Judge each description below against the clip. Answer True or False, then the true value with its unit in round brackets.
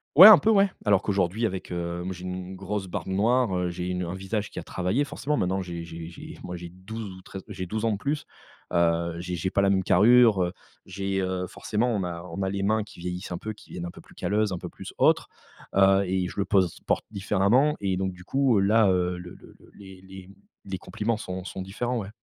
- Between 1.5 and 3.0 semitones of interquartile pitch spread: True (2.7 semitones)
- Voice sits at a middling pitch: False (95 Hz)